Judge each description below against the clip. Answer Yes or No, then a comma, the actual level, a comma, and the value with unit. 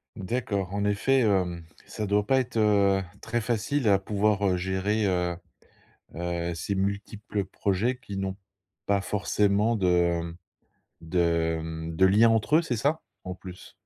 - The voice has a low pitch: Yes, low, 100 Hz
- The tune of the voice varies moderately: Yes, average, 3.0 semitones